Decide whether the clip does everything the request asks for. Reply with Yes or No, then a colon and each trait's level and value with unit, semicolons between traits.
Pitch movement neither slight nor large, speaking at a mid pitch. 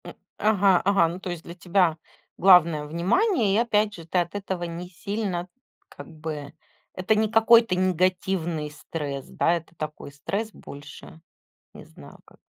Yes: average, 3.7 semitones; medium, 180 Hz